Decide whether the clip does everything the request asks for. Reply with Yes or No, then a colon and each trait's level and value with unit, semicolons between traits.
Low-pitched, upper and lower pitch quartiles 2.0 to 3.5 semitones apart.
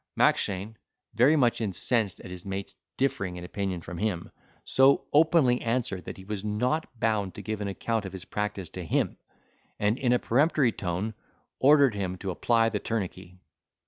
No: low, 105 Hz; average, 4.3 semitones